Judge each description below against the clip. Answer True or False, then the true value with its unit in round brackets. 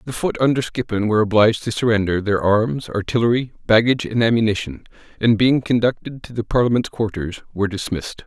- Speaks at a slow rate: False (165 wpm)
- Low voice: True (110 Hz)